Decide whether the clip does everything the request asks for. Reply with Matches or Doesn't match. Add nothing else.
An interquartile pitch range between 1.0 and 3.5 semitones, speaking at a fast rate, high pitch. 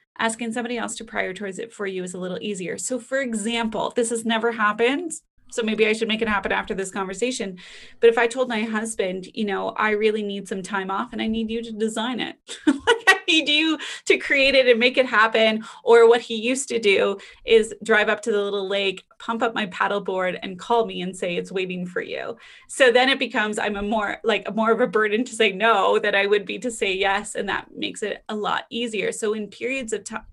Matches